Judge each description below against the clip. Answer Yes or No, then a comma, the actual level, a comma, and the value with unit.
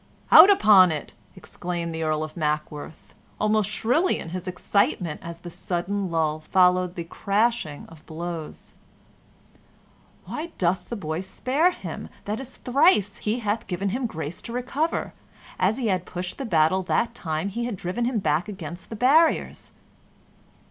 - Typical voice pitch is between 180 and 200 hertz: Yes, medium, 185 Hz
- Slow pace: No, average, 155 wpm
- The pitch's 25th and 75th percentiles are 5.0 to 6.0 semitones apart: Yes, wide, 5.6 semitones